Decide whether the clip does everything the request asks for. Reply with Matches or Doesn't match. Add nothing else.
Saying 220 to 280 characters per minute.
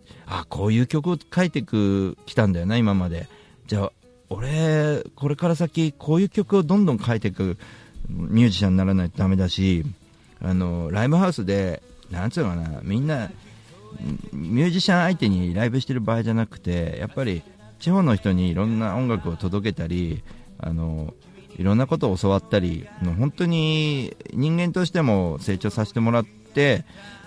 Doesn't match